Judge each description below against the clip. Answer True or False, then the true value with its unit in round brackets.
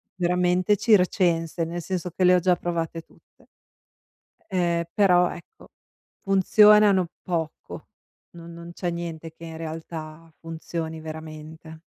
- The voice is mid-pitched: True (170 Hz)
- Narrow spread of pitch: True (1.9 semitones)